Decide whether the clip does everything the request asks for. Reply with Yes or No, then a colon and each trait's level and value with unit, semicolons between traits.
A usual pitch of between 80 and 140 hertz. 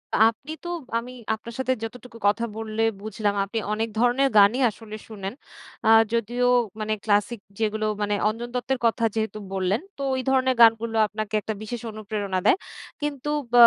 No: high, 225 Hz